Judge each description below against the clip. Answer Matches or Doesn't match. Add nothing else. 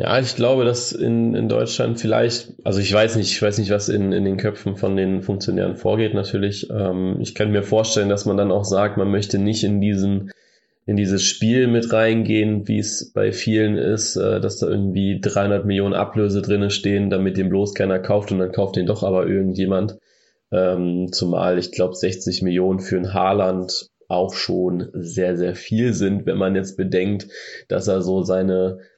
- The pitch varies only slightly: Matches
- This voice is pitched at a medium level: Doesn't match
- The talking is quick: Matches